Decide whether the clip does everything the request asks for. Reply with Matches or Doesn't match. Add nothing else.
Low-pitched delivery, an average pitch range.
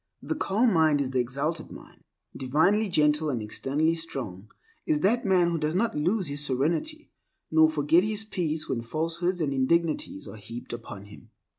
Doesn't match